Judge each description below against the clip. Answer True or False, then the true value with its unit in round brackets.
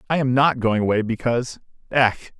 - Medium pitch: False (120 Hz)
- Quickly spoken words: False (175 wpm)